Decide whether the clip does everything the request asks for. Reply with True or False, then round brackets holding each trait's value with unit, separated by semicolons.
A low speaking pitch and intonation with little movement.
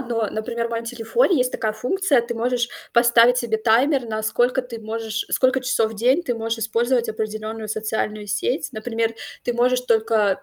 False (230 Hz; 2.1 semitones)